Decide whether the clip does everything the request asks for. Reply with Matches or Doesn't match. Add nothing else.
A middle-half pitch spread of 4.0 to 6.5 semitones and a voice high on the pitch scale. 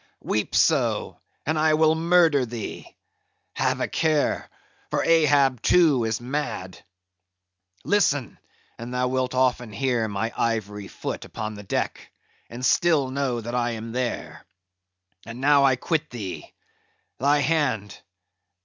Doesn't match